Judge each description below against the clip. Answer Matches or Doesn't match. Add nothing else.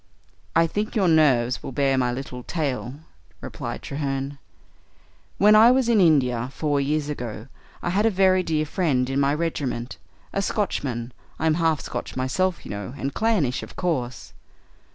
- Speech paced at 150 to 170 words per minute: Matches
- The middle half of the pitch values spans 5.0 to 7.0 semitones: Matches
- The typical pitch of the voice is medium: Matches